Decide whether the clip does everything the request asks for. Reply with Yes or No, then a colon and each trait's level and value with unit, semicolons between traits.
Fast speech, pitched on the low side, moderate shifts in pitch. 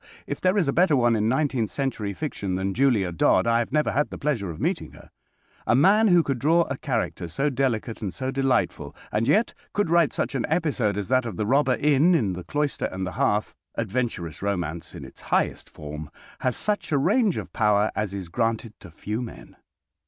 No: fast, 210 wpm; low, 120 Hz; wide, 6.3 semitones